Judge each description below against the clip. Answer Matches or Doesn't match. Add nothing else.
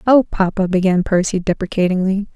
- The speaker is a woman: Matches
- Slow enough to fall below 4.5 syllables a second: Doesn't match